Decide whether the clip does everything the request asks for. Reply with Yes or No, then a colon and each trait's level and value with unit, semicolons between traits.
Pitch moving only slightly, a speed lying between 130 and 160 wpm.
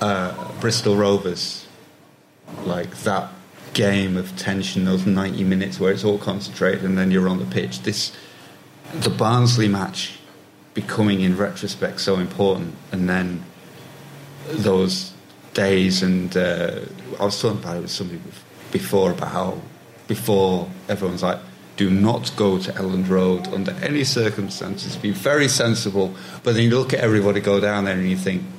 Yes: narrow, 1.9 semitones; average, 155 wpm